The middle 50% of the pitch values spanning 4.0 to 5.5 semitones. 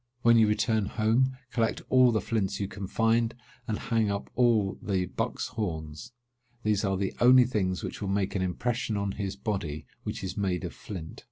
No: average, 3.0 semitones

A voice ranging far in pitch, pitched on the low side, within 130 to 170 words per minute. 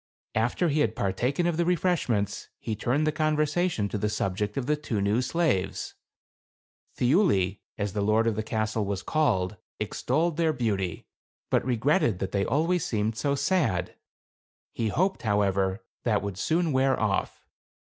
Yes: wide, 7.1 semitones; low, 115 Hz; average, 155 wpm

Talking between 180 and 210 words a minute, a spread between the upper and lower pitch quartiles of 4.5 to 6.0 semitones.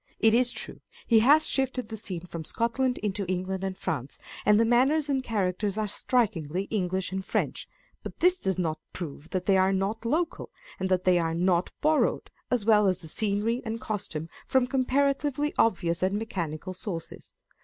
Yes: average, 185 wpm; average, 4.9 semitones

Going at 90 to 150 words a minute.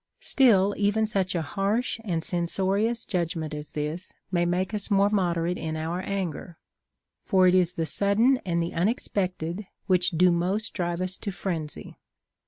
No: average, 165 wpm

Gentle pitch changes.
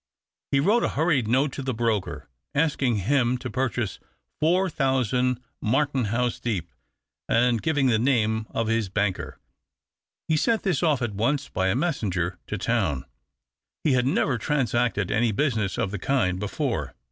No: average, 4.5 semitones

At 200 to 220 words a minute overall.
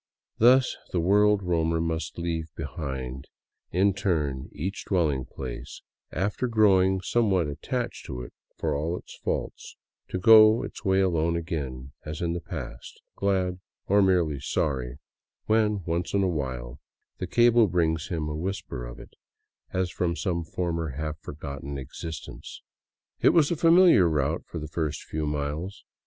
No: average, 155 wpm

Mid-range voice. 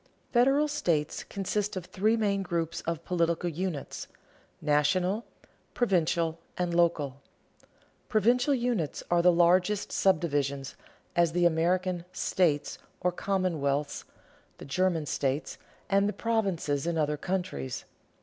Yes: medium, 175 Hz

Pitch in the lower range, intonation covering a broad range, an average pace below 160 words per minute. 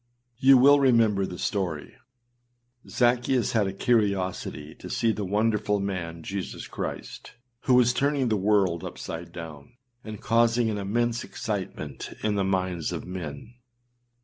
No: low, 105 Hz; average, 4.3 semitones; average, 140 wpm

